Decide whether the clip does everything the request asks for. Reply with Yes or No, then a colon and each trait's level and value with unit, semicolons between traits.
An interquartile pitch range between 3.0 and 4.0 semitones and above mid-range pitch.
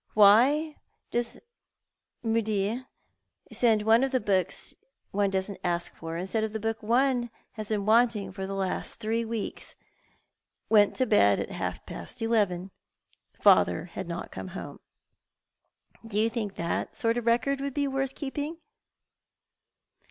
Yes: average, 3.4 semitones; high, 220 Hz